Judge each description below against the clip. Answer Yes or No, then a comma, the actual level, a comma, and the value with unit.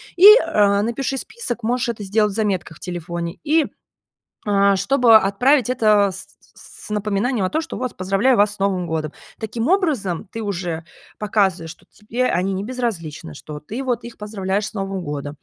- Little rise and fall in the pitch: No, average, 4.4 semitones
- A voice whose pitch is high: Yes, high, 205 Hz